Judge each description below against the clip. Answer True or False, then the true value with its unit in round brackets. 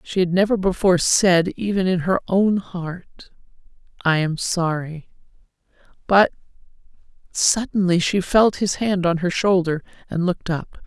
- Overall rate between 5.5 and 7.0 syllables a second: False (4.4 syllables/s)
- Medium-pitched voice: True (180 Hz)